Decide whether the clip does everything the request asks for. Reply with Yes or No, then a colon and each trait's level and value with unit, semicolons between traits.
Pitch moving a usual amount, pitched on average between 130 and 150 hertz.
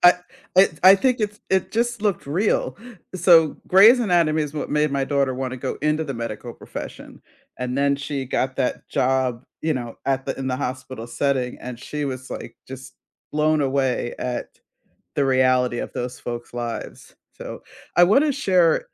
Yes: average, 5.0 semitones; medium, 140 Hz